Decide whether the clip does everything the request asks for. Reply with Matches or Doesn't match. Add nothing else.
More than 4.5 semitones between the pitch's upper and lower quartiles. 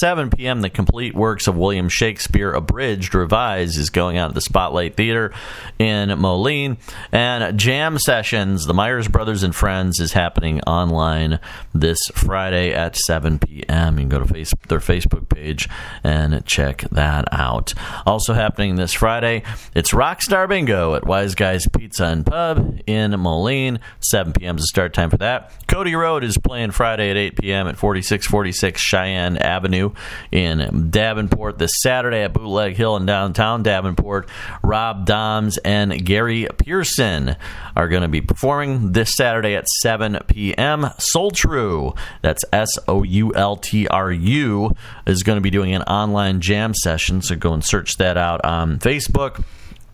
Doesn't match